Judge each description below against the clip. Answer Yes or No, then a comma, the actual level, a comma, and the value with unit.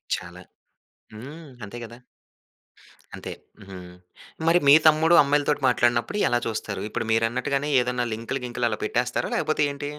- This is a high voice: No, low, 125 Hz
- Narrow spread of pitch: No, average, 4.2 semitones